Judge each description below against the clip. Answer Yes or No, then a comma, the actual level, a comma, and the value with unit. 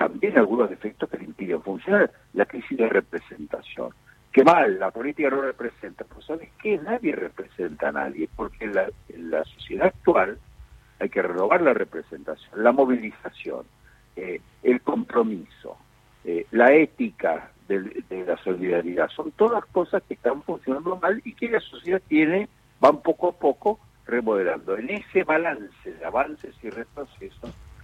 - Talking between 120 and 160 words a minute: Yes, average, 155 wpm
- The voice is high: No, medium, 140 Hz